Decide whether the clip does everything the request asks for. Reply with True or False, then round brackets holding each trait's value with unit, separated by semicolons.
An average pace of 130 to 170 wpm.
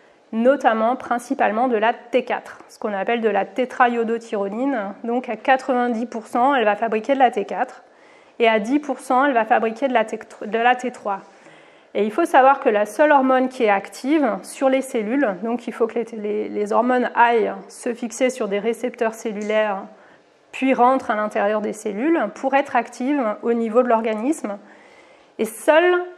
True (165 wpm)